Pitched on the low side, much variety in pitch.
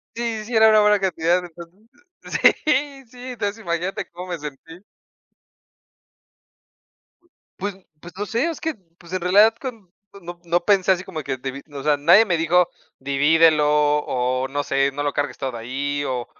No: medium, 170 Hz; wide, 6.0 semitones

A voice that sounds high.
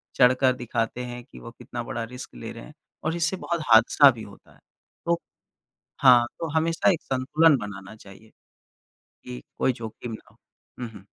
No: low, 120 Hz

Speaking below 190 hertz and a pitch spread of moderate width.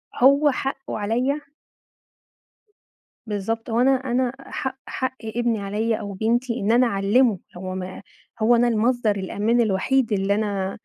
No: high, 230 Hz; average, 3.8 semitones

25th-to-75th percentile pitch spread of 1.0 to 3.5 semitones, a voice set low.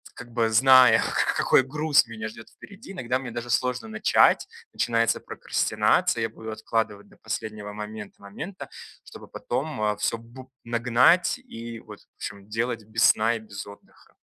Yes: average, 2.7 semitones; low, 115 Hz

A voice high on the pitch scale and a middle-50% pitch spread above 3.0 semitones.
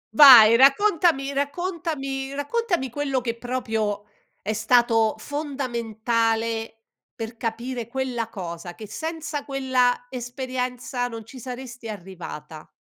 Yes: high, 245 Hz; average, 3.4 semitones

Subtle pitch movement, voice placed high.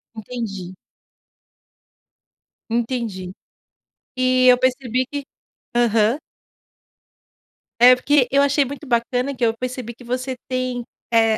Yes: narrow, 2.0 semitones; very high, 250 Hz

